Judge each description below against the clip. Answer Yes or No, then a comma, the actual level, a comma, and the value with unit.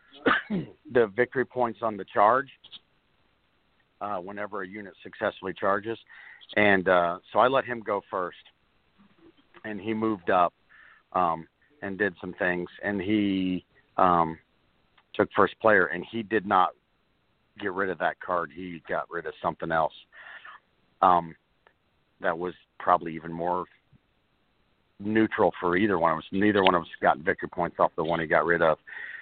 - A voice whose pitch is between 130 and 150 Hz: No, very low, 95 Hz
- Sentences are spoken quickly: No, average, 155 wpm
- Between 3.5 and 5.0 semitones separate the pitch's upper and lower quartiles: Yes, average, 4.0 semitones